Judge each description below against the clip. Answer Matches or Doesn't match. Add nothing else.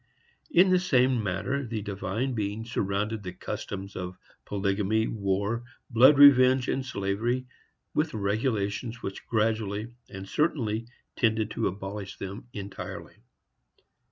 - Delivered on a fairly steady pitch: Doesn't match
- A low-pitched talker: Matches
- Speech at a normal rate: Doesn't match